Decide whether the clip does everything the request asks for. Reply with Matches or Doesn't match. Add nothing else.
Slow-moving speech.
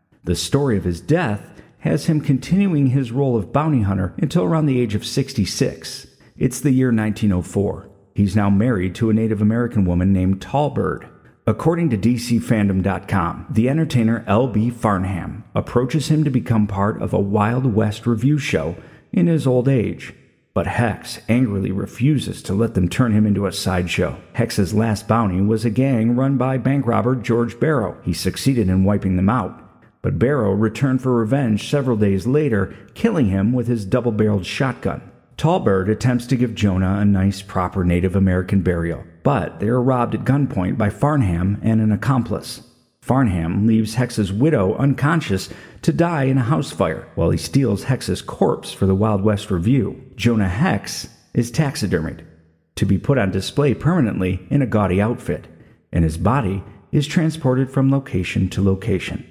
Doesn't match